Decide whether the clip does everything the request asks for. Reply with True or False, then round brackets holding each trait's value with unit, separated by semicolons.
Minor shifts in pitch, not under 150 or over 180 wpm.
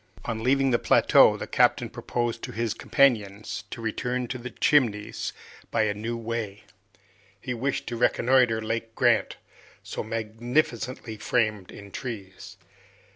False (2.3 semitones; 135 wpm)